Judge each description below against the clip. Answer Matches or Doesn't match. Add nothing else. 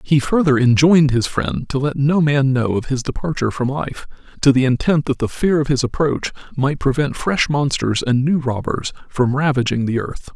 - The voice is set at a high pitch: Doesn't match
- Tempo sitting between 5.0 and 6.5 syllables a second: Matches